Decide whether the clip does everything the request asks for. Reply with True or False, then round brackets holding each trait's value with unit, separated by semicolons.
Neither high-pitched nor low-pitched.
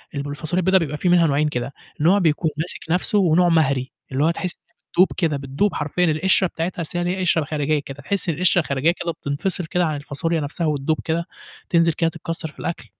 True (165 Hz)